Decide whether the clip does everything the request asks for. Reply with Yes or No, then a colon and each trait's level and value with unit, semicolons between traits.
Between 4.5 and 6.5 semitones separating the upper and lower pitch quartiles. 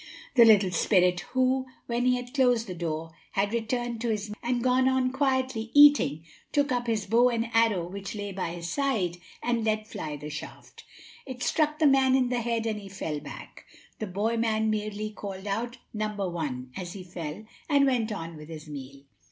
Yes: average, 5.3 semitones